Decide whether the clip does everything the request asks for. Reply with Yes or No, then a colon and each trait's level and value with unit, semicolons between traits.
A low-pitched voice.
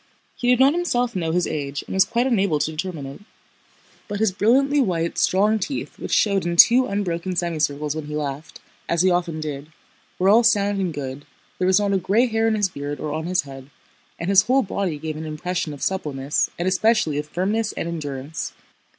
No: medium, 180 Hz